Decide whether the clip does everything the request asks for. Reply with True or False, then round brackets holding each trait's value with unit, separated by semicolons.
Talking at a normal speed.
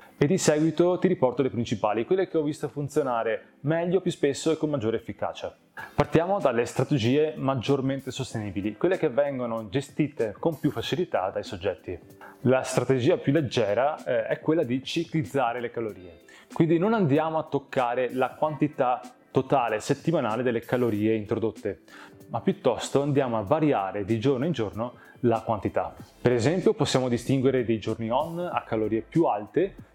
True (155 wpm)